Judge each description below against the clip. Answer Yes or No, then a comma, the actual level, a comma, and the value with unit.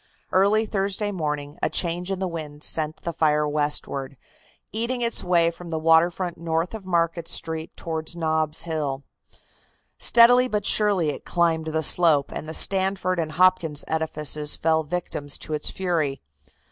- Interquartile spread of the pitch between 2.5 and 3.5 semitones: Yes, average, 3.1 semitones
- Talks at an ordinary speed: Yes, average, 160 wpm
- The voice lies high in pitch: No, medium, 165 Hz